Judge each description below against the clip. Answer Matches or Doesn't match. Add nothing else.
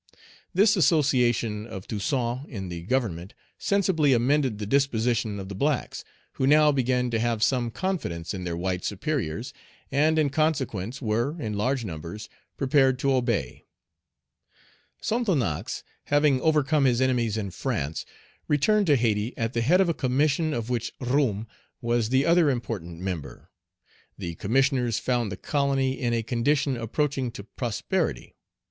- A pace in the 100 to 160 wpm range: Matches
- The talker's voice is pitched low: Matches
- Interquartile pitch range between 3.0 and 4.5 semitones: Doesn't match